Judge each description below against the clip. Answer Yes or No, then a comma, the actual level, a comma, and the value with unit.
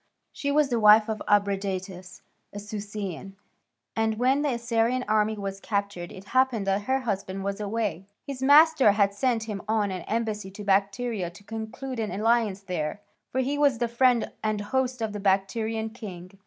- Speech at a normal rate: Yes, average, 175 wpm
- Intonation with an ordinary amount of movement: Yes, average, 3.2 semitones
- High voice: Yes, high, 215 Hz